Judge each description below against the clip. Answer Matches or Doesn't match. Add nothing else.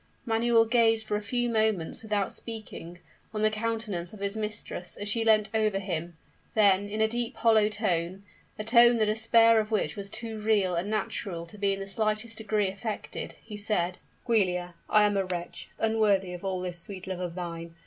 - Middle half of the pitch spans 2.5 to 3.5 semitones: Matches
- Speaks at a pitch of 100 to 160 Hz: Doesn't match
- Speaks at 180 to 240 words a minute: Matches